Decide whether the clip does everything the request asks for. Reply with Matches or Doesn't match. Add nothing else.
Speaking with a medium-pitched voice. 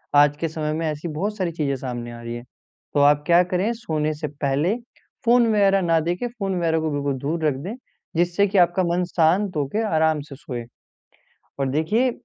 Matches